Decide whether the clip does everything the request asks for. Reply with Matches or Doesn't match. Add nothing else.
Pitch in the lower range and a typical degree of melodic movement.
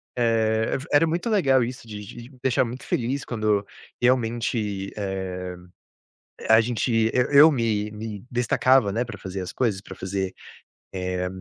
Matches